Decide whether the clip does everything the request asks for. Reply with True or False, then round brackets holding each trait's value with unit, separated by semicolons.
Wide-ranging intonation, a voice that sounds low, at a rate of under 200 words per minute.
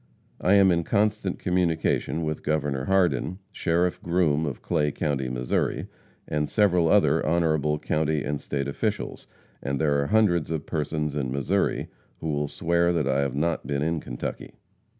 False (3.1 semitones; 80 Hz; 160 wpm)